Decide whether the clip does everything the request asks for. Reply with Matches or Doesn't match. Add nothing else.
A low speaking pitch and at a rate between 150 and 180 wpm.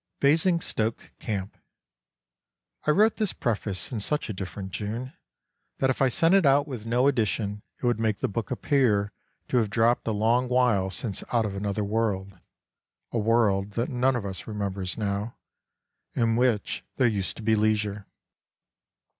Matches